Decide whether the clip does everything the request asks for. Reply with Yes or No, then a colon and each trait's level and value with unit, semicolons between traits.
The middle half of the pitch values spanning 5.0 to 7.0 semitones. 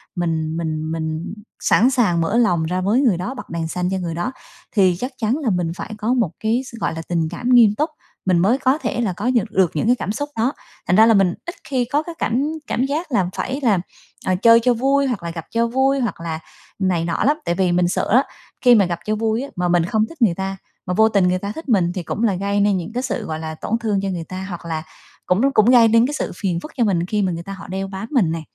Yes: wide, 5.4 semitones